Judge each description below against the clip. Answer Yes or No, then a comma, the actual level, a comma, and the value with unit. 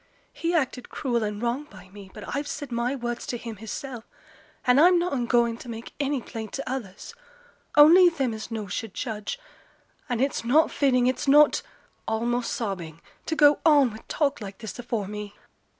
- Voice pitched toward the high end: Yes, high, 240 Hz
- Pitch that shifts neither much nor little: Yes, average, 4.3 semitones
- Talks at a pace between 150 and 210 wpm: Yes, average, 180 wpm